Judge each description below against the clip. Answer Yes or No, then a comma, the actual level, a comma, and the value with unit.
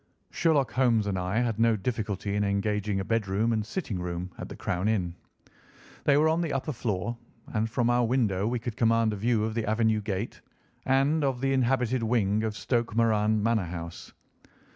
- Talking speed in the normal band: Yes, average, 190 wpm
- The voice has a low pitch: Yes, low, 110 Hz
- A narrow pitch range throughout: No, average, 3.0 semitones